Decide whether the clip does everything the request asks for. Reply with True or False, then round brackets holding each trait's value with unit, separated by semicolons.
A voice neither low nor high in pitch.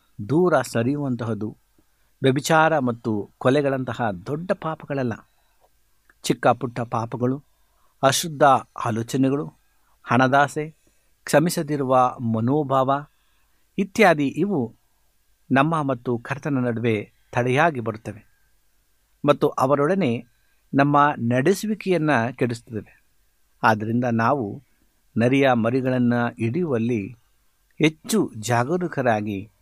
False (125 Hz)